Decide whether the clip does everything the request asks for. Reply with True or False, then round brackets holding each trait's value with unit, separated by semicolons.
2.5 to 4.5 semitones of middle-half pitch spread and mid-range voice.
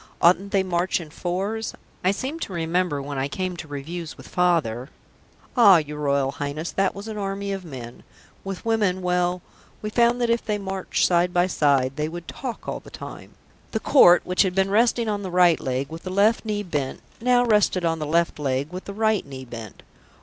False (5.0 semitones; 180 Hz)